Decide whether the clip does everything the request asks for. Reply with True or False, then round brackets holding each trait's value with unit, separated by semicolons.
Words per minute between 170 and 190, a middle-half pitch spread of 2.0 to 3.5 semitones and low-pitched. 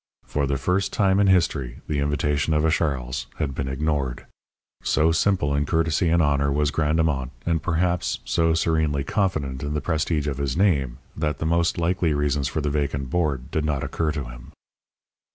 True (185 wpm; 2.8 semitones; 75 Hz)